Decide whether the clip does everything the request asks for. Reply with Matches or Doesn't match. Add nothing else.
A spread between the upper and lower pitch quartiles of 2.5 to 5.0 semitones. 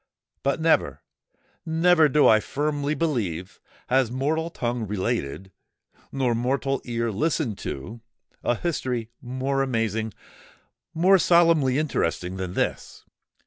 Doesn't match